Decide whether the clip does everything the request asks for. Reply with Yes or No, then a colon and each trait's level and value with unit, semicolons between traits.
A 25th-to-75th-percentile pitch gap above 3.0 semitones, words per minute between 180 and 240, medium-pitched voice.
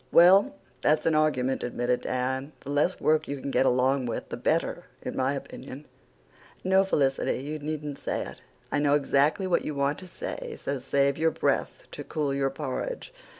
No: narrow, 2.6 semitones; average, 185 wpm; medium, 145 Hz